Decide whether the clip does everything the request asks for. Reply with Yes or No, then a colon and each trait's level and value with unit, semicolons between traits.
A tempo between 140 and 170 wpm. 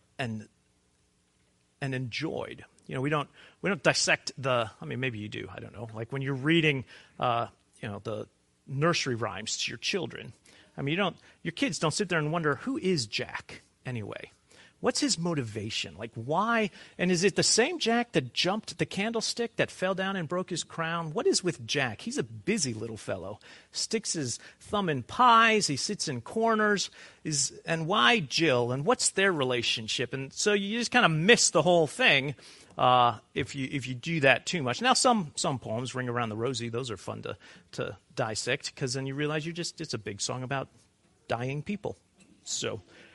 No: average, 195 wpm